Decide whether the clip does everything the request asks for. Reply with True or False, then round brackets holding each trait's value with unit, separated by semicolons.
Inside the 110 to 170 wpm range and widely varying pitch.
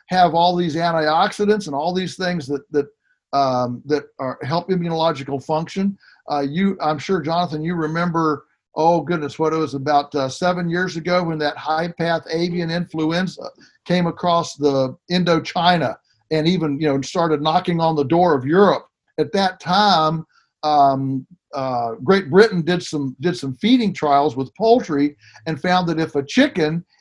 False (165 wpm; 3.6 semitones)